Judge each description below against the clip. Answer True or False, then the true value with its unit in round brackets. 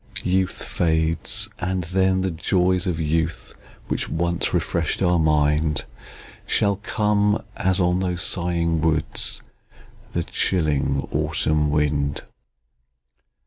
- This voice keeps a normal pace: False (105 wpm)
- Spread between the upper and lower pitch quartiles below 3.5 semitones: True (3.1 semitones)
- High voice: False (85 Hz)